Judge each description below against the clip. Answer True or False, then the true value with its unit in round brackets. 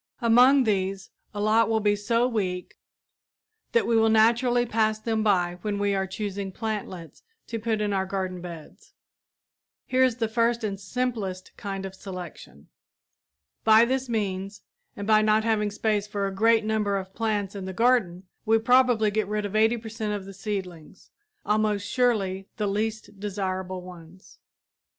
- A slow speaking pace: False (165 wpm)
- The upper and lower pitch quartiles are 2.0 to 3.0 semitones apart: True (2.7 semitones)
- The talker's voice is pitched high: True (210 Hz)